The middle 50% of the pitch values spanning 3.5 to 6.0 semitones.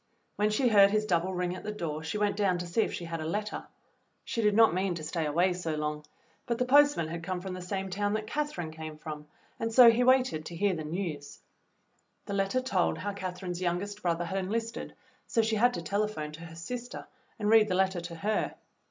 Yes: average, 4.0 semitones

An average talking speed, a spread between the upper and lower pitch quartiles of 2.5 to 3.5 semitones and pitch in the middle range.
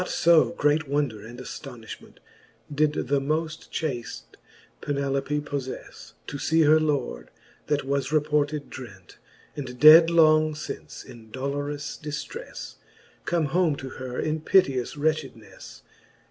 No: slow, 125 wpm; average, 2.9 semitones; medium, 145 Hz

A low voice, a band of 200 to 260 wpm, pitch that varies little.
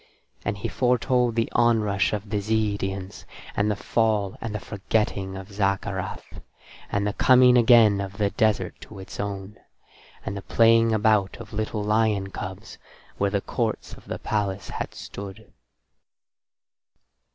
No: low, 105 Hz; average, 145 wpm; narrow, 2.1 semitones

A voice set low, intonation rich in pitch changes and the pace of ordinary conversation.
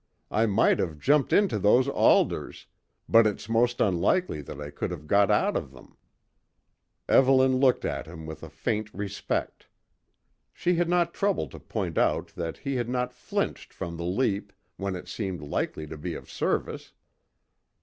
Yes: low, 105 Hz; wide, 7.2 semitones; average, 170 wpm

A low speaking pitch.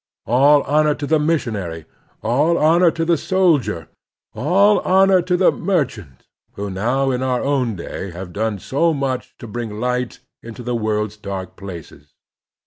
Yes: low, 125 Hz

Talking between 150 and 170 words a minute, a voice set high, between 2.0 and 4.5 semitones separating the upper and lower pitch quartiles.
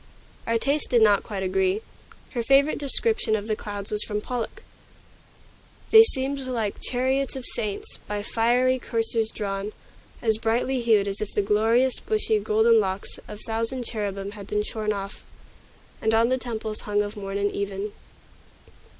Yes: average, 160 wpm; high, 220 Hz; average, 3.2 semitones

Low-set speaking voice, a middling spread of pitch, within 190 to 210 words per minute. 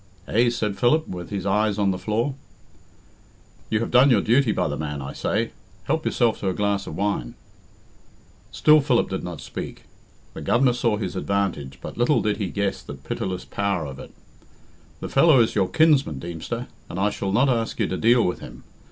Yes: low, 105 Hz; average, 4.4 semitones; average, 195 wpm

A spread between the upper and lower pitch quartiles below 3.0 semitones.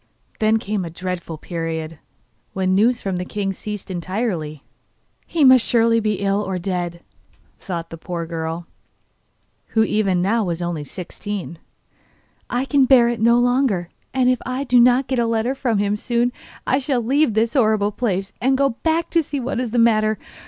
No: average, 5.2 semitones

